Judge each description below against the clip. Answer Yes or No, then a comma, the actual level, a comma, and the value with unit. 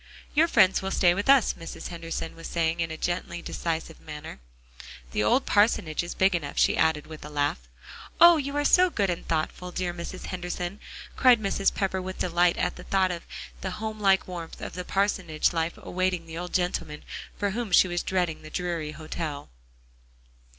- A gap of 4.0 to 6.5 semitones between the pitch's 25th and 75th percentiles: No, average, 2.9 semitones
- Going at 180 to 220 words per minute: Yes, average, 185 wpm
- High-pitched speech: No, medium, 175 Hz